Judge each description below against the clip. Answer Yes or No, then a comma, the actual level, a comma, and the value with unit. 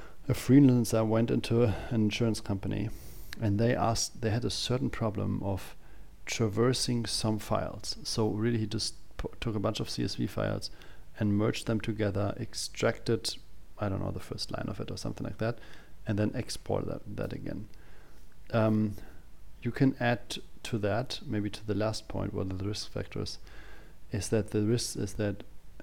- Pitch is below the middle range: Yes, low, 110 Hz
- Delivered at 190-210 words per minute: No, average, 170 wpm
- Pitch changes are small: Yes, narrow, 2.3 semitones